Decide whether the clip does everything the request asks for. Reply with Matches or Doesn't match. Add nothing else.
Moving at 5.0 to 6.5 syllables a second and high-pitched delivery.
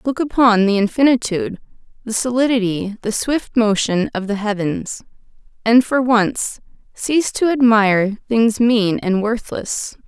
Doesn't match